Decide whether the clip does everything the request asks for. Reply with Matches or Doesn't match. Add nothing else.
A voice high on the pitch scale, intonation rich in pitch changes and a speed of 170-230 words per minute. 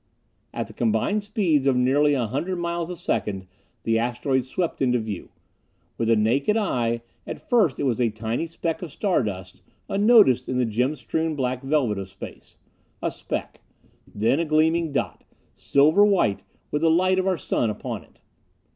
Doesn't match